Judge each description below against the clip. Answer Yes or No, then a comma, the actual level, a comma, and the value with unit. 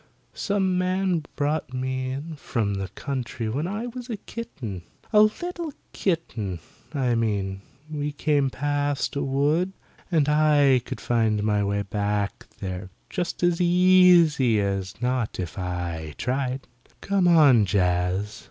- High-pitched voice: No, low, 135 Hz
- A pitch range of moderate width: No, wide, 8.5 semitones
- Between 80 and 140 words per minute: Yes, slow, 135 wpm